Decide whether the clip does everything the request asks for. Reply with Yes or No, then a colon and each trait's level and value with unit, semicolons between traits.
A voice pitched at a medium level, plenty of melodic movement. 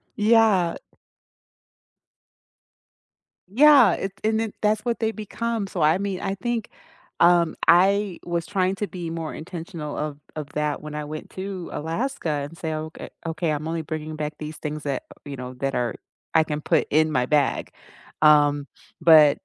No: medium, 165 Hz; average, 4.5 semitones